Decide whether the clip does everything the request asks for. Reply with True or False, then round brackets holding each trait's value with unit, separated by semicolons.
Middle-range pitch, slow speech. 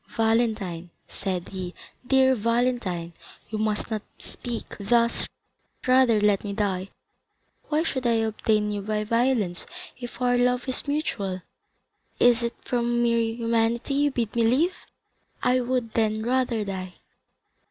False (230 Hz; 130 wpm)